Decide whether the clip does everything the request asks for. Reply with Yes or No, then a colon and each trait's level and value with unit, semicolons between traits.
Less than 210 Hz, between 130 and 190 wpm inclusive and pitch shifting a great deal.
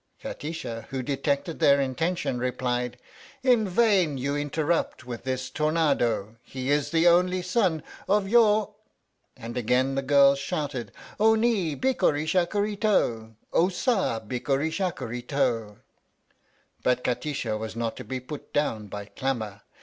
Yes: medium, 140 Hz; average, 140 wpm; wide, 6.2 semitones